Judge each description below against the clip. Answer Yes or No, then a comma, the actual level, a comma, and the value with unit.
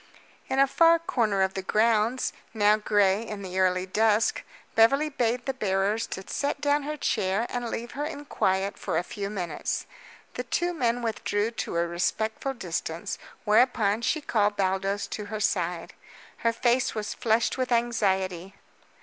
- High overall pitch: Yes, high, 215 Hz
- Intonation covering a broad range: No, average, 4.1 semitones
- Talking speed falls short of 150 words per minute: No, average, 165 wpm